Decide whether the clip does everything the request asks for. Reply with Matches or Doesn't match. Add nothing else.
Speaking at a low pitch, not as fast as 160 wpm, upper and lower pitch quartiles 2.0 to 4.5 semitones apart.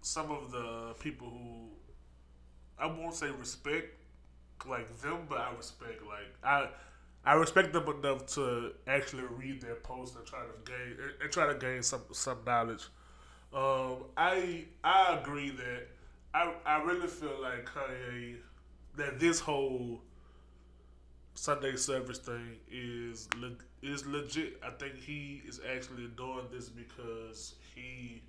Matches